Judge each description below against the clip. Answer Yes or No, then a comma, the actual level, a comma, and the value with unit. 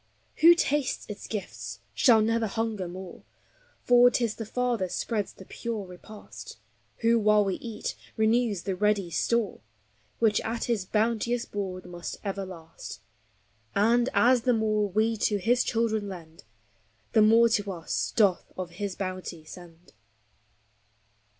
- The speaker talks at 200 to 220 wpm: No, average, 145 wpm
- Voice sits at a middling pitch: No, high, 210 Hz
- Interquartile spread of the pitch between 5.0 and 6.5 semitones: No, average, 3.6 semitones